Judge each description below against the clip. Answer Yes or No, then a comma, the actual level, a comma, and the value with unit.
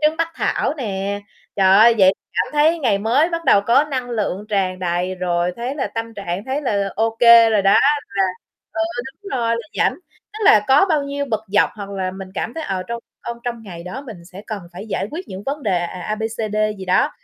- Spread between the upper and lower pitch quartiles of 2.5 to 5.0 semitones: No, wide, 5.6 semitones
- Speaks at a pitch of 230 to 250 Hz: No, high, 220 Hz